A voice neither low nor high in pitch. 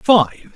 Yes: medium, 175 Hz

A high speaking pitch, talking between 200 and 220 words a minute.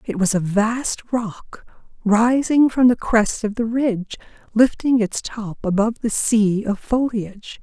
No: high, 220 Hz; average, 155 wpm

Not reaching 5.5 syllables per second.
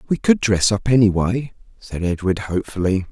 Yes: 5.3 syllables/s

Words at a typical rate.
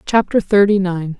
Yes: average, 150 wpm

